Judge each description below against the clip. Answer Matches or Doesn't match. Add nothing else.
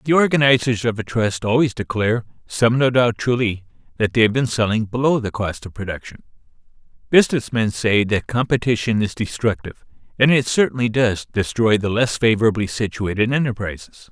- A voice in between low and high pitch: Doesn't match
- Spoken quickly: Doesn't match